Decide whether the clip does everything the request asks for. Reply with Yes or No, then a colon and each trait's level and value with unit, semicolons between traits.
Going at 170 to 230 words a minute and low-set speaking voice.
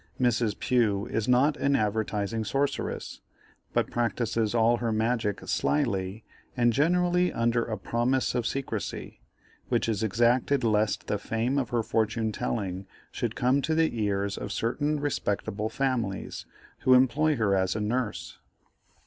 No: average, 140 wpm; low, 115 Hz